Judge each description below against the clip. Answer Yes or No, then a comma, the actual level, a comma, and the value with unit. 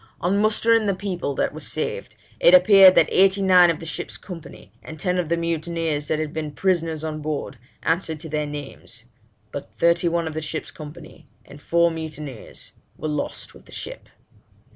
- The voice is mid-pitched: Yes, medium, 165 Hz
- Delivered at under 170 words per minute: No, average, 185 wpm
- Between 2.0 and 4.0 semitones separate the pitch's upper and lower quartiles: Yes, average, 2.9 semitones